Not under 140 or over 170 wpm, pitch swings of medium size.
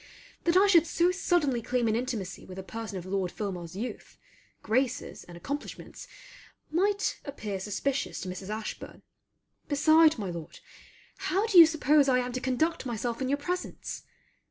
No: average, 160 wpm; wide, 7.3 semitones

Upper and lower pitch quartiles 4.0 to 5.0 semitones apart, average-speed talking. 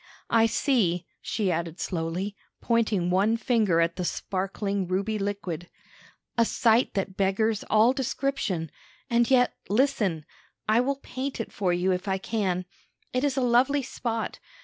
Yes: average, 4.5 semitones; average, 150 wpm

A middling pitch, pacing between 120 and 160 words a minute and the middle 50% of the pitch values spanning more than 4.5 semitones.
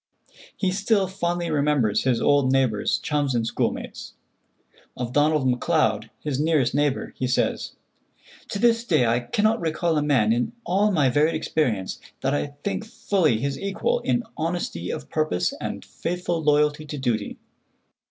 Yes: medium, 150 Hz; average, 155 wpm; wide, 5.4 semitones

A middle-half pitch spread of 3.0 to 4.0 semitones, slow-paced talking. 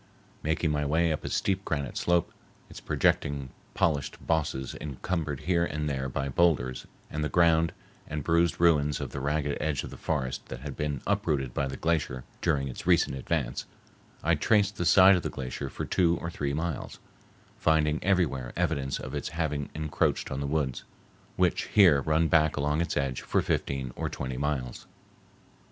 No: average, 3.3 semitones; average, 175 wpm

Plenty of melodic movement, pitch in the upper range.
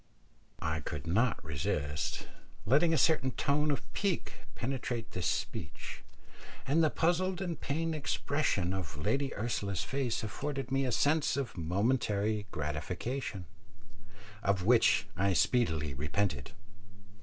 No: wide, 7.7 semitones; low, 115 Hz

